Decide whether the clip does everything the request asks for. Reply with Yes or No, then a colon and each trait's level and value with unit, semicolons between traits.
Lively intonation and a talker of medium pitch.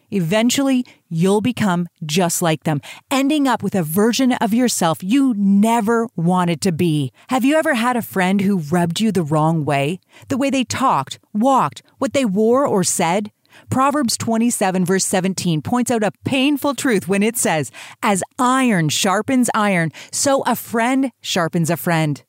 No: wide, 6.1 semitones; high, 205 Hz